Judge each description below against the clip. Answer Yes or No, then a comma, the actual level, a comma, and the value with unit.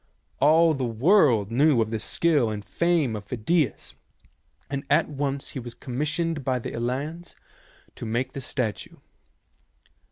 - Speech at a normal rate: Yes, average, 150 wpm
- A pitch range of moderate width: Yes, average, 4.7 semitones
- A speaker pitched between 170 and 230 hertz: No, low, 135 Hz